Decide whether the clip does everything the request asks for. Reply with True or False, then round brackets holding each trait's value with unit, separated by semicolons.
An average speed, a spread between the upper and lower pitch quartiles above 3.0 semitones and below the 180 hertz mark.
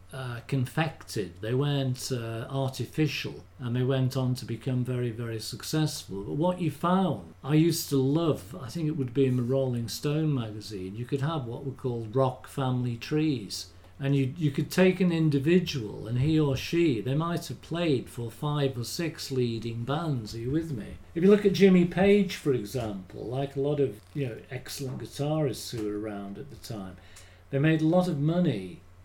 True (195 wpm; 4.7 semitones; 135 Hz)